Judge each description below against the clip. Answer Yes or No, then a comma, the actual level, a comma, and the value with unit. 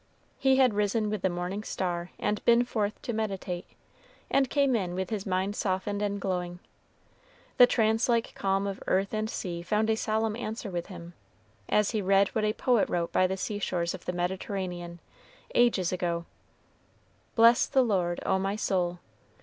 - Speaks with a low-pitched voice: No, high, 200 Hz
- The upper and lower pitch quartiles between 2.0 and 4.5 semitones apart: Yes, average, 3.3 semitones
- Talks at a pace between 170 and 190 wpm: Yes, average, 175 wpm